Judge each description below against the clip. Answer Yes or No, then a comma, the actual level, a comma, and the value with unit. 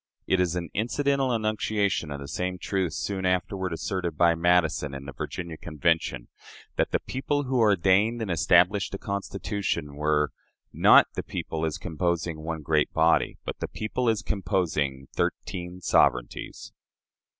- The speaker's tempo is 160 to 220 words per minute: No, average, 150 wpm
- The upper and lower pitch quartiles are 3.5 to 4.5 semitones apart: Yes, average, 4.0 semitones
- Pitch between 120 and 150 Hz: No, very low, 90 Hz